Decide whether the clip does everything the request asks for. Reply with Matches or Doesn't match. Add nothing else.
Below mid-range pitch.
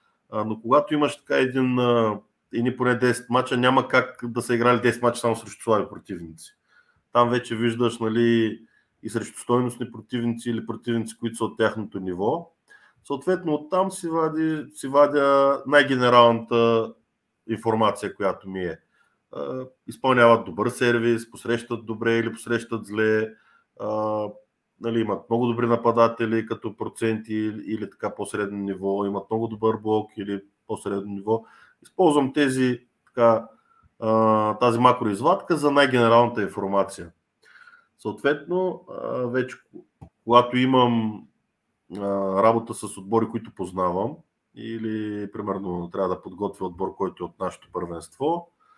Matches